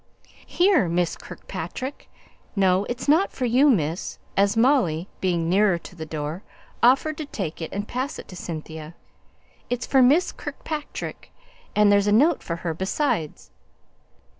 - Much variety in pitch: Yes, wide, 7.8 semitones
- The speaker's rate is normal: Yes, average, 150 wpm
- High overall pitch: Yes, high, 200 Hz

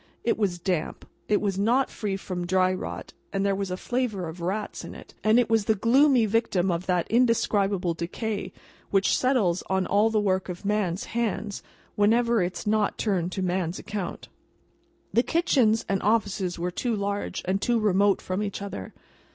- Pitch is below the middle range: No, high, 200 Hz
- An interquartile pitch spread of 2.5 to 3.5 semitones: Yes, average, 3.1 semitones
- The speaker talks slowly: No, average, 175 wpm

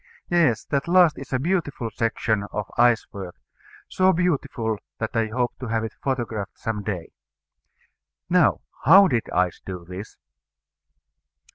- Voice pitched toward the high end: No, low, 115 Hz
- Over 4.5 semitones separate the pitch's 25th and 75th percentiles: Yes, average, 4.9 semitones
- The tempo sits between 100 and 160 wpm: Yes, average, 140 wpm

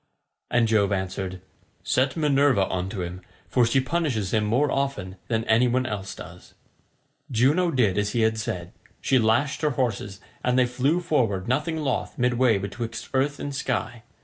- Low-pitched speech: Yes, low, 120 Hz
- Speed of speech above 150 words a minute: Yes, average, 170 wpm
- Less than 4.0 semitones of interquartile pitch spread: No, average, 5.0 semitones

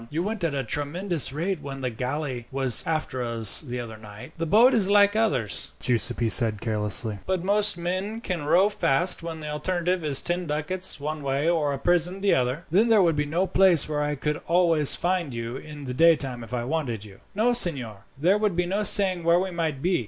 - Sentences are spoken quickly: Yes, fast, 215 wpm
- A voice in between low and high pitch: Yes, medium, 155 Hz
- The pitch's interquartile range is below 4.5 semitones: No, wide, 5.6 semitones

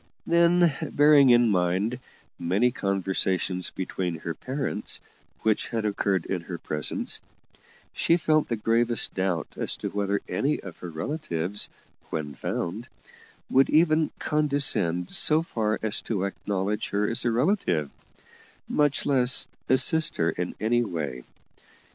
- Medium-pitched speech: No, low, 105 Hz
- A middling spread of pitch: No, wide, 7.2 semitones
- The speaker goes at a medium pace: No, slow, 130 wpm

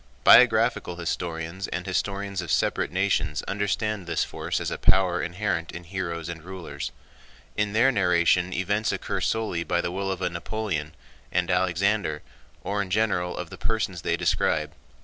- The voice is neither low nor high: No, very low, 90 Hz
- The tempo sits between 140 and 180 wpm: Yes, average, 160 wpm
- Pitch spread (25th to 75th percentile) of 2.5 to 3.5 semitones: Yes, average, 2.8 semitones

